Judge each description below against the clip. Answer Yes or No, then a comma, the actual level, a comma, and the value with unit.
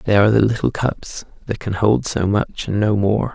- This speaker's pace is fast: Yes, fast, 235 wpm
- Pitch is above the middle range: No, low, 105 Hz